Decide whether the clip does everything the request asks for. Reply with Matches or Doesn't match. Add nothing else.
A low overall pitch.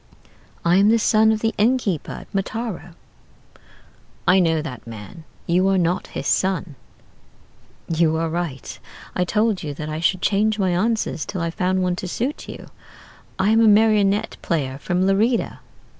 Doesn't match